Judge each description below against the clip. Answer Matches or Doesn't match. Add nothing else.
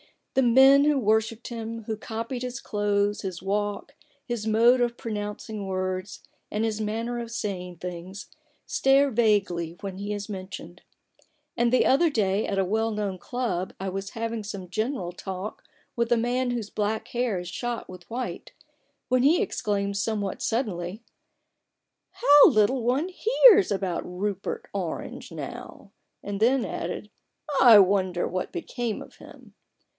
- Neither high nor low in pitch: Doesn't match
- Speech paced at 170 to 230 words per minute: Doesn't match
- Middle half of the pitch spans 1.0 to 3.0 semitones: Doesn't match